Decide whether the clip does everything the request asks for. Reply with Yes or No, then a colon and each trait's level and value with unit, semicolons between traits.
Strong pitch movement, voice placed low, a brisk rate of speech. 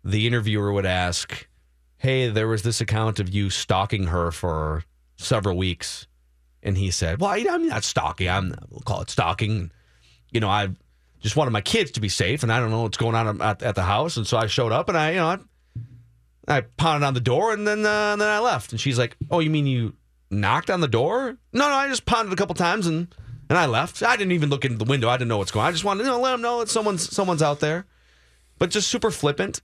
Yes: wide, 8.9 semitones; low, 115 Hz; fast, 255 wpm